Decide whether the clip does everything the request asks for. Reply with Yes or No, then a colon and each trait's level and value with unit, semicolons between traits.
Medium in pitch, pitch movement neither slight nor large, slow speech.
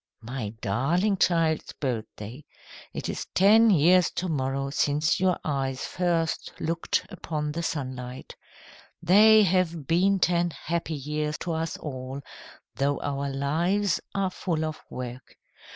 Yes: medium, 155 Hz; average, 4.4 semitones; slow, 130 wpm